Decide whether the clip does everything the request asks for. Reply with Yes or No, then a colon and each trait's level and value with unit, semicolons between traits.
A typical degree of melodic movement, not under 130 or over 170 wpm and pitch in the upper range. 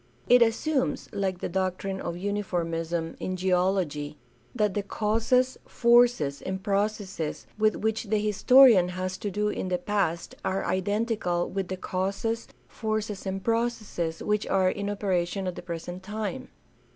Yes: average, 3.1 semitones; average, 145 wpm; high, 195 Hz